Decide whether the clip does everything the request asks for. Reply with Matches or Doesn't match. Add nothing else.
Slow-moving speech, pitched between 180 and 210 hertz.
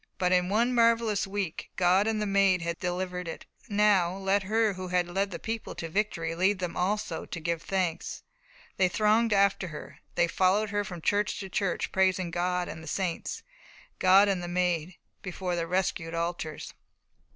Doesn't match